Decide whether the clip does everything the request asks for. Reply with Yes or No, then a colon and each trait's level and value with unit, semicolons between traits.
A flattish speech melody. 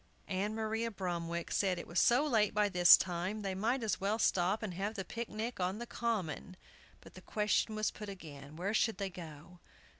No: average, 3.4 semitones